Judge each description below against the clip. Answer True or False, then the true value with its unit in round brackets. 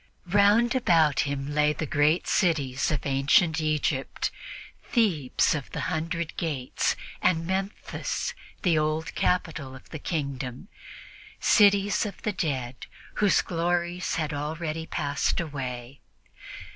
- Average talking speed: False (120 wpm)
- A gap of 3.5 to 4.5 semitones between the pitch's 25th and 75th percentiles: True (3.8 semitones)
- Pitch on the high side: False (155 Hz)